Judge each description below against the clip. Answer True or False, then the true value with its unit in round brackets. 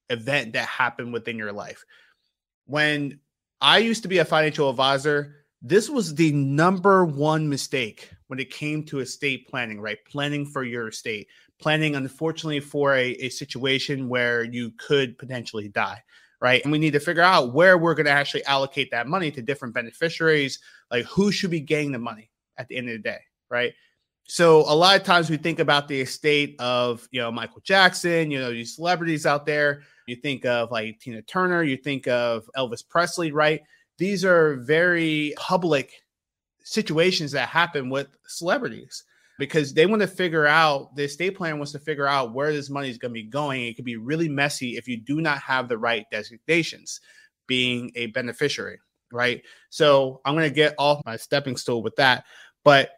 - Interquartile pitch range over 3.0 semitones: True (4.1 semitones)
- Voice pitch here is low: False (145 Hz)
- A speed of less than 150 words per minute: False (185 wpm)